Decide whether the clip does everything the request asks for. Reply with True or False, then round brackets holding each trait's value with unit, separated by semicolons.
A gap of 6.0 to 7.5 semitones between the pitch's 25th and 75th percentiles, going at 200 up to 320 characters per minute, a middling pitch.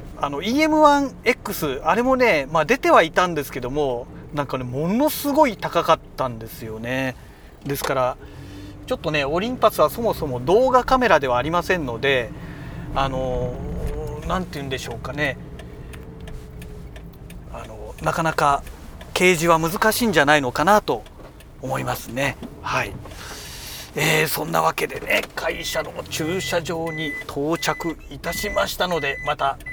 True (7.0 semitones; 295 characters per minute; 155 Hz)